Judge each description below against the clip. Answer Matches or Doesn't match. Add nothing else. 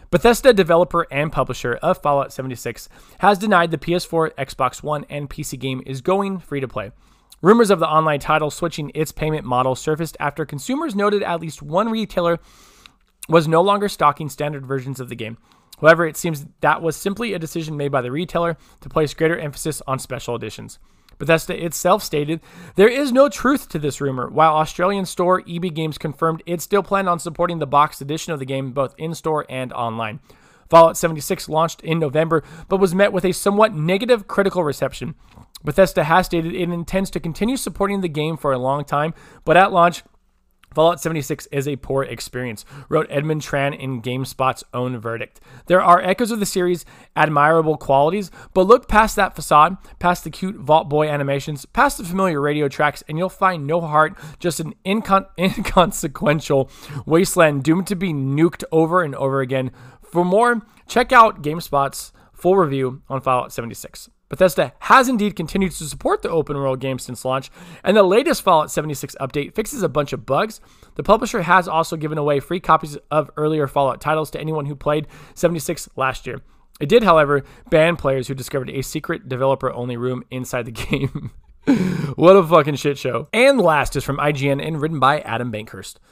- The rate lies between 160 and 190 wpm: Matches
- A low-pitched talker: Doesn't match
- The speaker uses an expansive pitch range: Doesn't match